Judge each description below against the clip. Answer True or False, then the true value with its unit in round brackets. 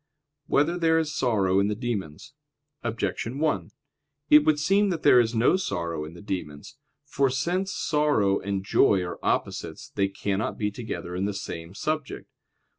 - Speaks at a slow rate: False (170 wpm)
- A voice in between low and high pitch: False (115 Hz)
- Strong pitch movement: True (7.5 semitones)